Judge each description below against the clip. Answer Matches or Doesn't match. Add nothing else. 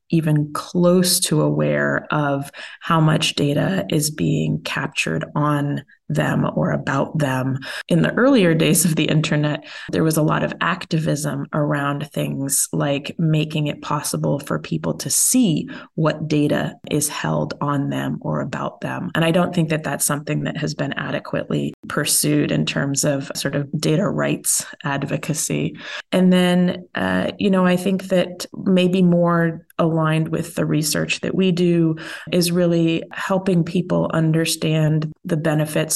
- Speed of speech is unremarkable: Matches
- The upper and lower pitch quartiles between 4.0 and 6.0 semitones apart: Doesn't match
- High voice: Doesn't match